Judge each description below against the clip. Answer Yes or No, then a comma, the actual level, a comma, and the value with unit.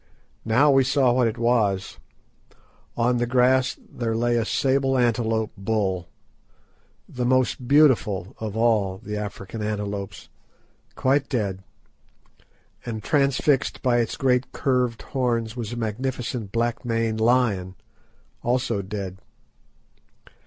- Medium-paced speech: No, slow, 110 wpm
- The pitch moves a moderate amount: Yes, average, 3.1 semitones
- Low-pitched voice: Yes, low, 115 Hz